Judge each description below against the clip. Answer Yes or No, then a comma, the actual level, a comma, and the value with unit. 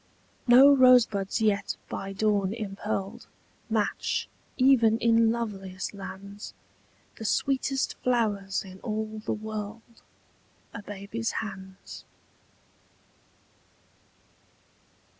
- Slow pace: Yes, slow, 85 wpm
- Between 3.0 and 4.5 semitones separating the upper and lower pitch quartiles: No, narrow, 2.6 semitones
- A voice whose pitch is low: No, high, 215 Hz